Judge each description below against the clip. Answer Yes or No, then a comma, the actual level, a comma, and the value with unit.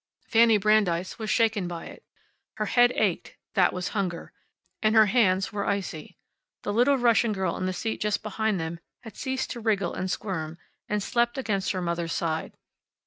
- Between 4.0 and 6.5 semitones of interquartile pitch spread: No, average, 3.6 semitones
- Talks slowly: No, average, 180 wpm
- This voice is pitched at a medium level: No, high, 205 Hz